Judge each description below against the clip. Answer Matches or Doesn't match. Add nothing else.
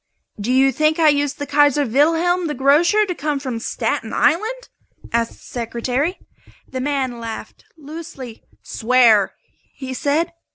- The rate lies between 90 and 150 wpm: Matches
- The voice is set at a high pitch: Matches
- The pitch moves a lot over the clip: Doesn't match